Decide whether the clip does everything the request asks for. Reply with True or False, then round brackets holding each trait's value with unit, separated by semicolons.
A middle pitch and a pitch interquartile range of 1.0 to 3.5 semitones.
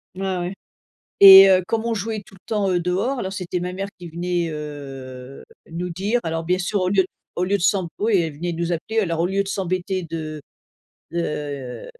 True (180 Hz; 2.9 semitones)